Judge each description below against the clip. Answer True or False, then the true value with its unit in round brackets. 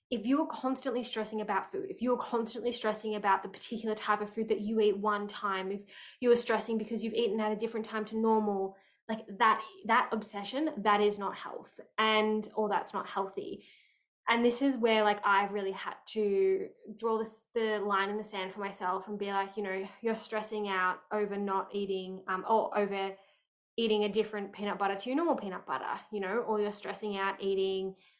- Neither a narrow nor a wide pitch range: False (2.2 semitones)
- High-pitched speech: True (215 Hz)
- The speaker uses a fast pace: True (210 wpm)